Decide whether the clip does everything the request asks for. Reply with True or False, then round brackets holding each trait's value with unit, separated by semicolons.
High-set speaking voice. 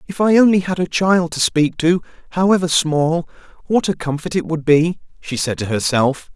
False (165 Hz)